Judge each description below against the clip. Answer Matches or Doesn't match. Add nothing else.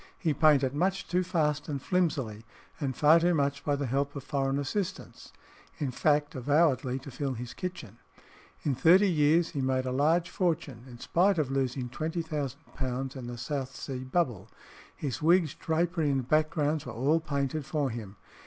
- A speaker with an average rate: Matches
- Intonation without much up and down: Doesn't match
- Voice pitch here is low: Doesn't match